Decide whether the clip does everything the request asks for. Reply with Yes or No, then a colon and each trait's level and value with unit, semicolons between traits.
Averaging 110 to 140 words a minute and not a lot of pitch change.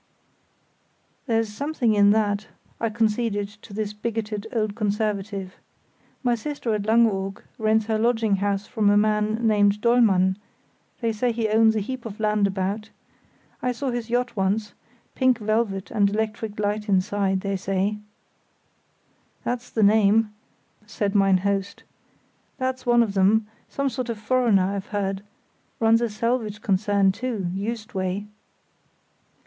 Yes: slow, 135 wpm; narrow, 2.2 semitones